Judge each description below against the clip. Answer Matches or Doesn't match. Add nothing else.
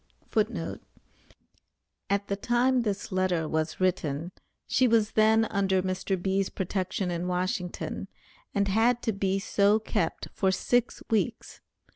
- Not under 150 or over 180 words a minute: Doesn't match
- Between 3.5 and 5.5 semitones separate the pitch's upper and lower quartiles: Doesn't match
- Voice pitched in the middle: Doesn't match